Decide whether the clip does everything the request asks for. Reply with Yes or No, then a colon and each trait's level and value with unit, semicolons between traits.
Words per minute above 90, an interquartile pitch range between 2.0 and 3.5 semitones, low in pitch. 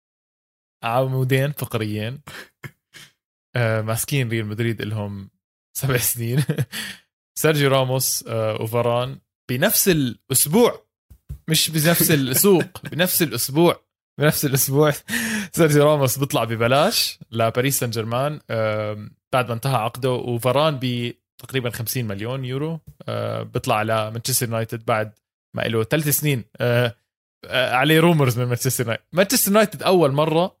No: average, 105 wpm; average, 4.7 semitones; low, 130 Hz